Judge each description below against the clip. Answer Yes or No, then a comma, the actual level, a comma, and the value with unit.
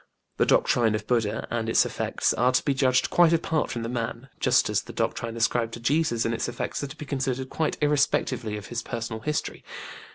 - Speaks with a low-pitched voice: Yes, low, 120 Hz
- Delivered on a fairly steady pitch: No, average, 3.3 semitones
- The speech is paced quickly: Yes, fast, 215 wpm